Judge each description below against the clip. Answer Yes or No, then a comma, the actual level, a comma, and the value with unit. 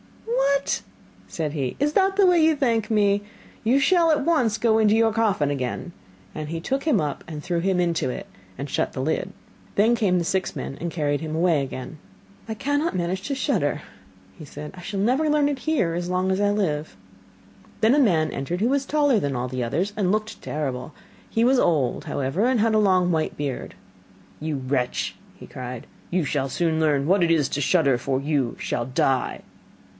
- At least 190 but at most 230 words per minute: Yes, average, 200 wpm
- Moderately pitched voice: Yes, medium, 180 Hz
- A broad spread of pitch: Yes, wide, 7.6 semitones